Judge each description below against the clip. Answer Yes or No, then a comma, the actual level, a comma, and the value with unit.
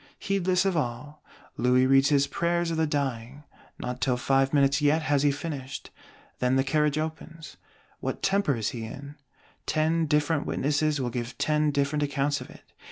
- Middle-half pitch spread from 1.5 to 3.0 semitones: Yes, narrow, 2.5 semitones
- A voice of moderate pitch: Yes, medium, 145 Hz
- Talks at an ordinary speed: Yes, average, 170 wpm